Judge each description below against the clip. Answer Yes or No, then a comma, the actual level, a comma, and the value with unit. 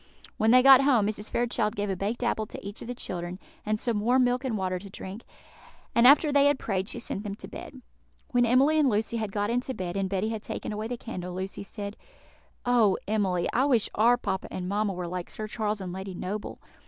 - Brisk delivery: Yes, fast, 230 wpm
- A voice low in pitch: No, high, 215 Hz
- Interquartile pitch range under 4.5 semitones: Yes, average, 3.9 semitones